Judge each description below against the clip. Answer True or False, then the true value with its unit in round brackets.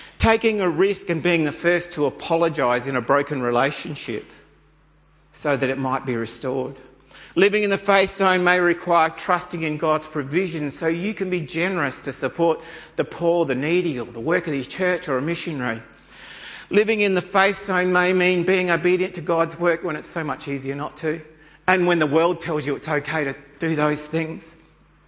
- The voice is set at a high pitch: False (165 Hz)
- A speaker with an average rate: True (195 wpm)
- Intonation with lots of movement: False (4.0 semitones)